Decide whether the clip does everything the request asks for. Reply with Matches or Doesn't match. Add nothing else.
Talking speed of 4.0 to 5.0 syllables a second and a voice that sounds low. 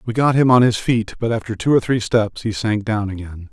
Doesn't match